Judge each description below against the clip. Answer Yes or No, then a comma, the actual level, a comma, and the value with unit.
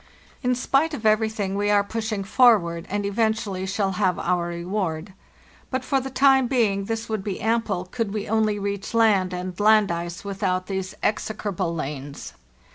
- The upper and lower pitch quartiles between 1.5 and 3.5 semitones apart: Yes, average, 3.1 semitones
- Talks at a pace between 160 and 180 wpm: Yes, average, 165 wpm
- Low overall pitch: No, high, 205 Hz